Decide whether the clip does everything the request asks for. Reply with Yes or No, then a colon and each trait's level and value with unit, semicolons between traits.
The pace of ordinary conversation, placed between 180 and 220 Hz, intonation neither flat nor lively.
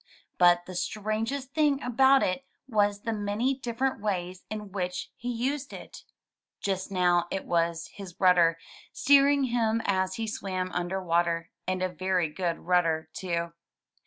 Yes: average, 155 wpm; high, 190 Hz; average, 4.5 semitones